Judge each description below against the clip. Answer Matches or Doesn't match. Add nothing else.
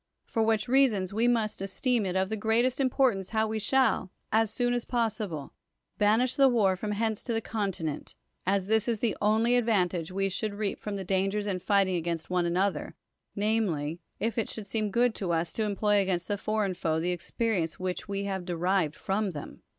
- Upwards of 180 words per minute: Matches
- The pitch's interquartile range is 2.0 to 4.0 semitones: Matches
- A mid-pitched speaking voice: Doesn't match